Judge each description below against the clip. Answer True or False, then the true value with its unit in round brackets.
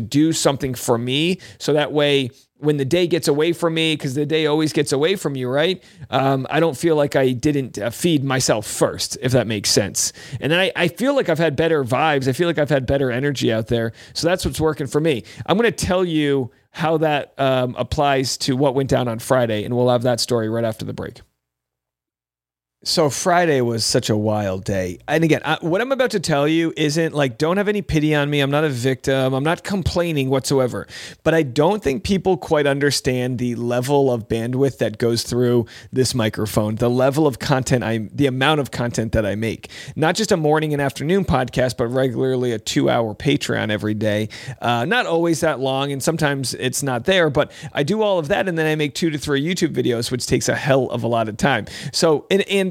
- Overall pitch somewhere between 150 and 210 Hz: False (135 Hz)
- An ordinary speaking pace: False (225 wpm)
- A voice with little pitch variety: False (4.4 semitones)